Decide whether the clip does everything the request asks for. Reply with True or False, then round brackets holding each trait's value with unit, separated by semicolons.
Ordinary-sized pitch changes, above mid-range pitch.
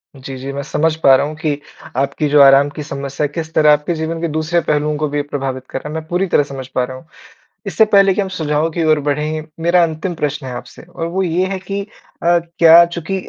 False (3.1 semitones; 155 Hz)